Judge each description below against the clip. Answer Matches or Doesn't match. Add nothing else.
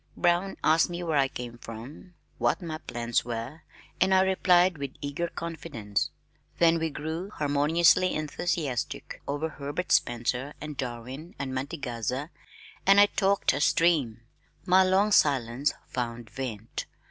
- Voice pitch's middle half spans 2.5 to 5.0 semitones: Doesn't match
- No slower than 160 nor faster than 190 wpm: Doesn't match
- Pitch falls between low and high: Matches